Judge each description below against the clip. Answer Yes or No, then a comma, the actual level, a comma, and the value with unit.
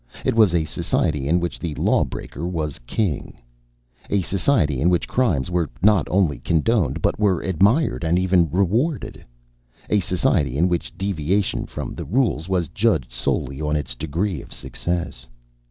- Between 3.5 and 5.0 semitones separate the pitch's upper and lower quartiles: Yes, average, 4.6 semitones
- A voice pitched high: No, very low, 85 Hz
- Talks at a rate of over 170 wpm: No, average, 155 wpm